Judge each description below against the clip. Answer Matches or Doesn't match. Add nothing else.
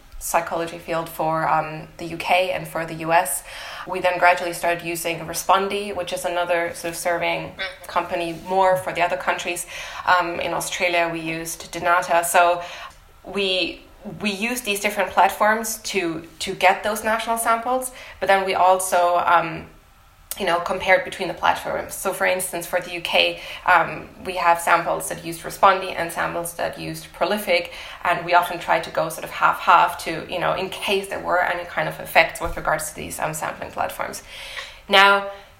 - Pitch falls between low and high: Matches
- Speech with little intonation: Matches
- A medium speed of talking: Matches